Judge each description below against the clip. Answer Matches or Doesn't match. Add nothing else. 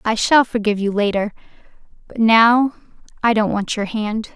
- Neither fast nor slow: Matches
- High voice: Matches